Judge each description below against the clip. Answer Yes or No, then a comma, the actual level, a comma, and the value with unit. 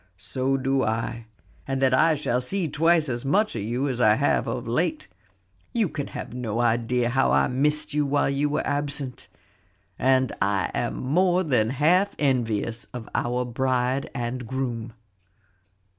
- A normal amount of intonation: Yes, average, 3.4 semitones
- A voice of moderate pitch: No, low, 130 Hz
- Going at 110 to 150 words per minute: No, average, 160 wpm